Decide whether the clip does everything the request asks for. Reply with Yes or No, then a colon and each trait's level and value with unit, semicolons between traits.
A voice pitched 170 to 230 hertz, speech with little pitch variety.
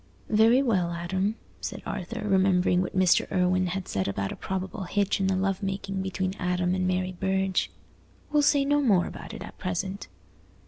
Yes: high, 190 Hz; narrow, 1.6 semitones